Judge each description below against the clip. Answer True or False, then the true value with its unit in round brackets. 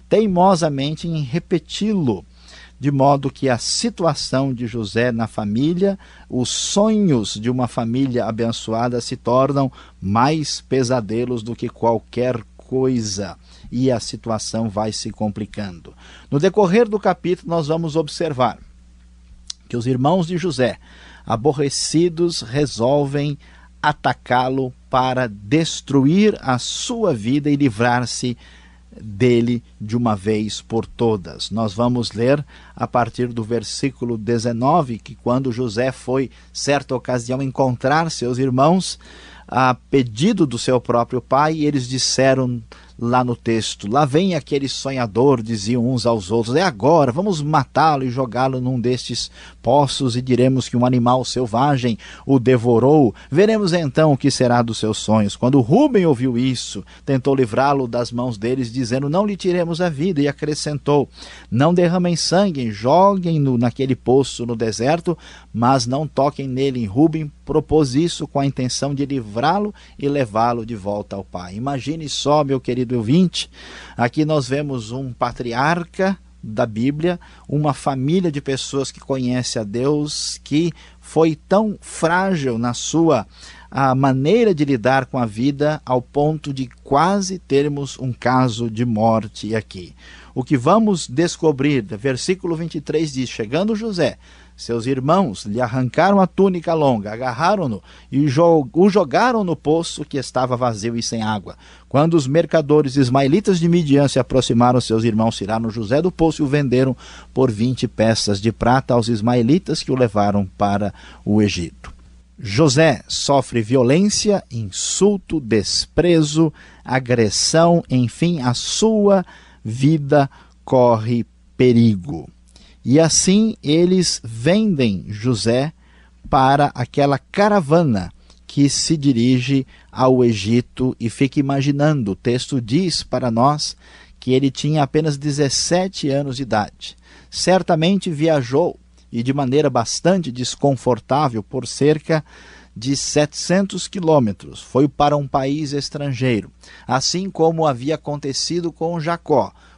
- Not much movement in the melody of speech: False (4.5 semitones)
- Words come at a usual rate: True (135 wpm)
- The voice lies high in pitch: False (130 Hz)